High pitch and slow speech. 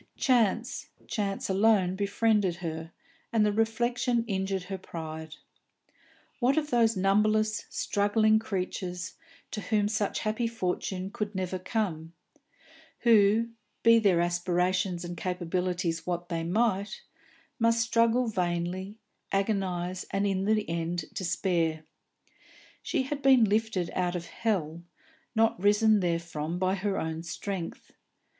Yes: high, 195 Hz; slow, 120 wpm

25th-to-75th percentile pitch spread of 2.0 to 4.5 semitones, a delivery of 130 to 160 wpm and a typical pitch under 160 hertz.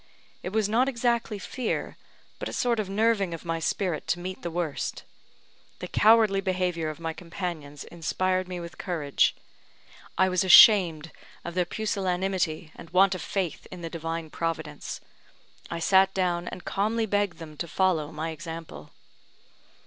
No: average, 2.9 semitones; average, 155 wpm; medium, 180 Hz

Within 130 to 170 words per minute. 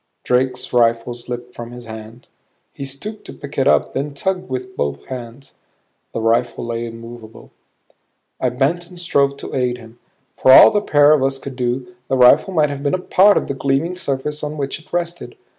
No: average, 195 wpm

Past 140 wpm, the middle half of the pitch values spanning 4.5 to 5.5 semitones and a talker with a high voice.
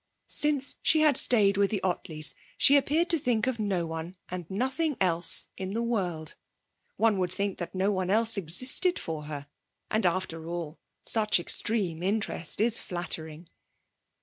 Yes: average, 160 wpm; average, 5.2 semitones; high, 195 Hz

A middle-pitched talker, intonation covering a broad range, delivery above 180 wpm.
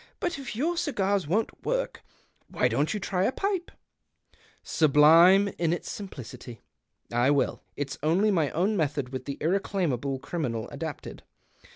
No: medium, 170 Hz; wide, 6.3 semitones; average, 155 wpm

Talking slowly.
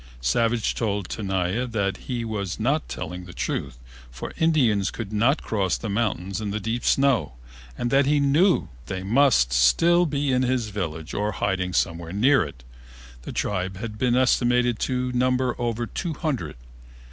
No: average, 165 wpm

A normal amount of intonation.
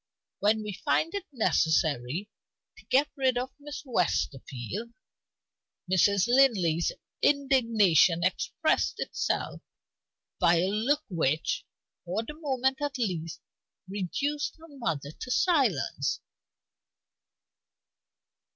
No: wide, 7.9 semitones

